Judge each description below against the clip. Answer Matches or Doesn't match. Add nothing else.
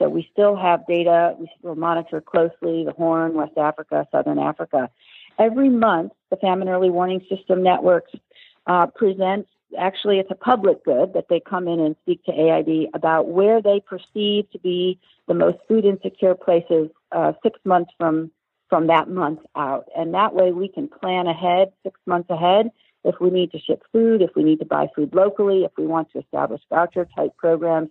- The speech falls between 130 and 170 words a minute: Doesn't match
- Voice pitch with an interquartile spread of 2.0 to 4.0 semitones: Matches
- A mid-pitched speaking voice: Matches